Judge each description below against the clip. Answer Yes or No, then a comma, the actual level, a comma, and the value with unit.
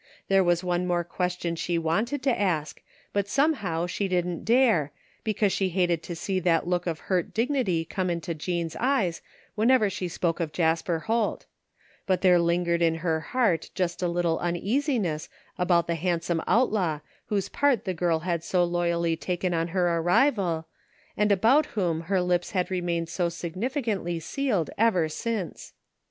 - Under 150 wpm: No, average, 165 wpm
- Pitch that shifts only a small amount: No, average, 3.1 semitones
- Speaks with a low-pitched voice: No, medium, 180 Hz